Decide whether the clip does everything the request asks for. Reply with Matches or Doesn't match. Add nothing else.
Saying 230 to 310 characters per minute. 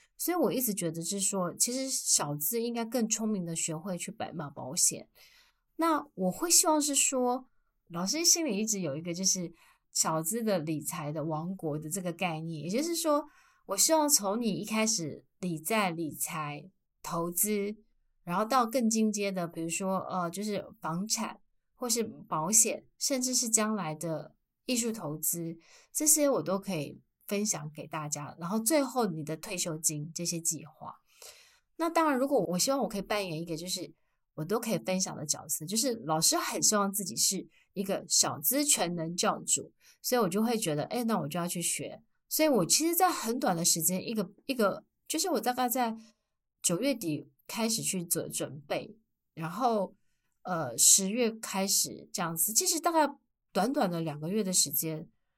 Matches